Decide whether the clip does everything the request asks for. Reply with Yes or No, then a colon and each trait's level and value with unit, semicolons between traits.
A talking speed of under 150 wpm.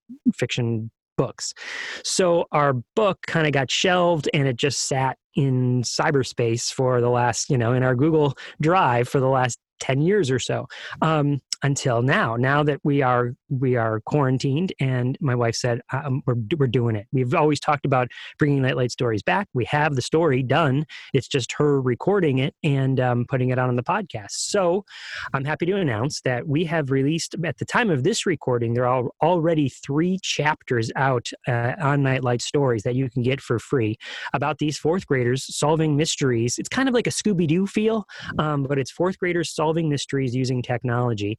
No: average, 190 wpm